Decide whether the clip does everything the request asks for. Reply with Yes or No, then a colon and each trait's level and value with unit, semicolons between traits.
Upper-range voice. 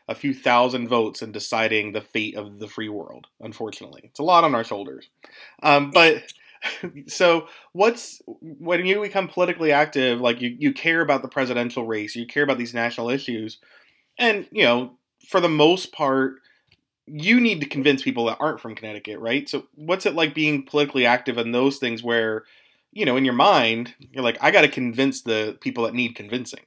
No: low, 135 Hz